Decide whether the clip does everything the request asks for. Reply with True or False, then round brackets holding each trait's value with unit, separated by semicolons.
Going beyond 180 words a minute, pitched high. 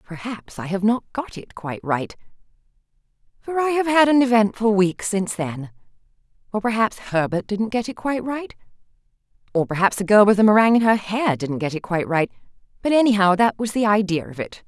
True (195 wpm; 210 Hz)